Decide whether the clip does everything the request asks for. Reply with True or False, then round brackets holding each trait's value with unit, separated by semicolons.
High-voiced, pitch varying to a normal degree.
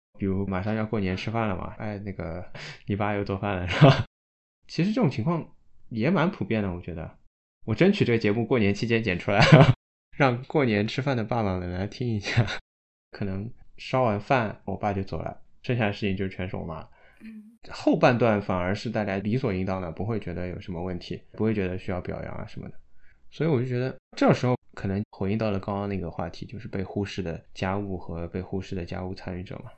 False (100 Hz; 4.2 semitones)